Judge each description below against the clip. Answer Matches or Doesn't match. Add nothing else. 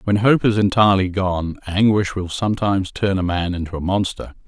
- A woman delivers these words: Doesn't match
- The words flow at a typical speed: Matches